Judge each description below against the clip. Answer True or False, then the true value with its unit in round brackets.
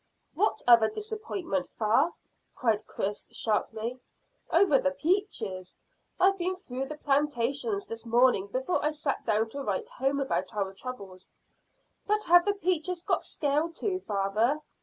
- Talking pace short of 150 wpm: True (140 wpm)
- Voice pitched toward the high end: True (275 Hz)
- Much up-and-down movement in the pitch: True (8.1 semitones)